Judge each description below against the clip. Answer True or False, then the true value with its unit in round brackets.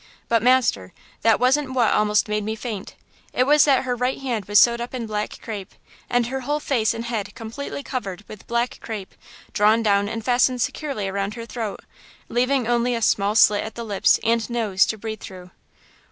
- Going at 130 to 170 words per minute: False (195 wpm)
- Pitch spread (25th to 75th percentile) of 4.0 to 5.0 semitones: False (2.9 semitones)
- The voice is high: True (230 Hz)